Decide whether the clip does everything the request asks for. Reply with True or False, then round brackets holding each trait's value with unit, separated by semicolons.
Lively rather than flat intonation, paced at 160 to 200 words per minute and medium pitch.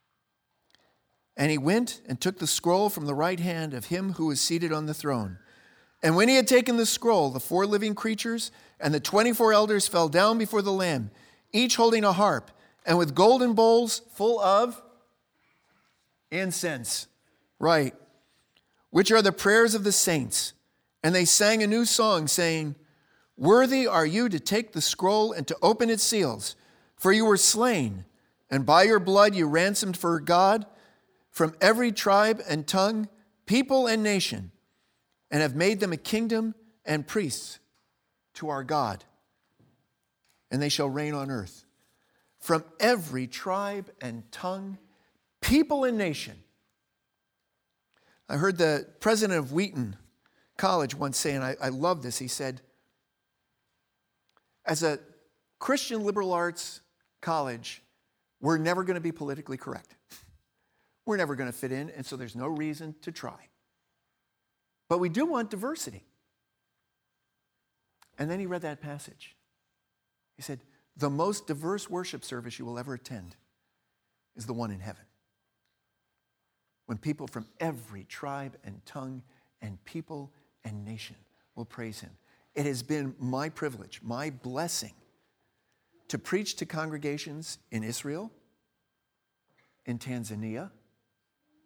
False (7.6 semitones; 145 wpm; 160 Hz)